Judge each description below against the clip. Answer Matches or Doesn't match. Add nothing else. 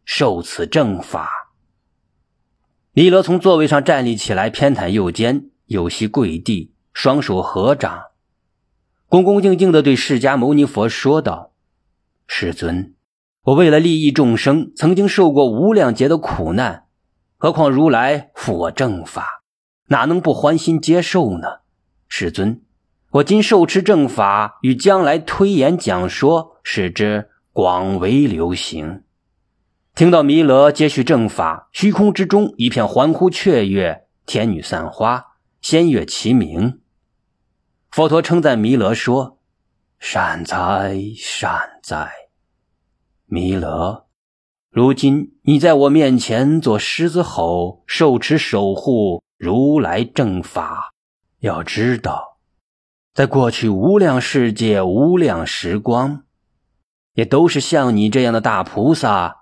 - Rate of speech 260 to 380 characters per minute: Doesn't match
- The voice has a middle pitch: Doesn't match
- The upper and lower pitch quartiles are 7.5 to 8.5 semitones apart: Matches